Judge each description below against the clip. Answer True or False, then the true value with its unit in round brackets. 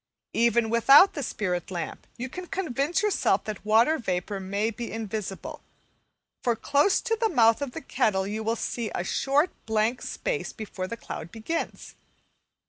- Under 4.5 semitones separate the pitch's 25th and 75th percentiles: False (5.1 semitones)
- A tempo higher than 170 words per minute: False (160 wpm)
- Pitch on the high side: True (230 Hz)